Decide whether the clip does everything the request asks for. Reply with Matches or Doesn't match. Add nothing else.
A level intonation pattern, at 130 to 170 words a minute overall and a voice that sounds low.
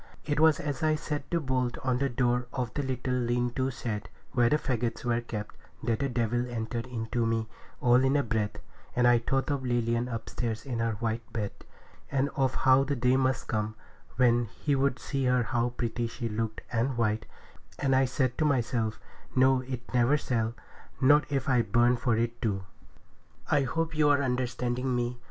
Doesn't match